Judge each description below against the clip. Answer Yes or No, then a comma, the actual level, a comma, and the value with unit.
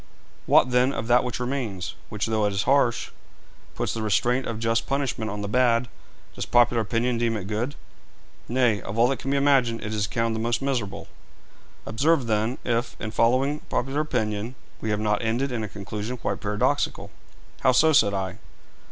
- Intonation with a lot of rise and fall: No, average, 2.8 semitones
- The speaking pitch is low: Yes, low, 115 Hz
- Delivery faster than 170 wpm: Yes, average, 185 wpm